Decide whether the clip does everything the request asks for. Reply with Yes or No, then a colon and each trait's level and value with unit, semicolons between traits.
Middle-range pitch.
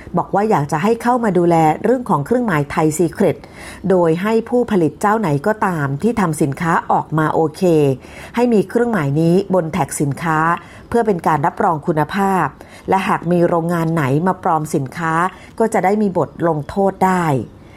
Yes: medium, 175 Hz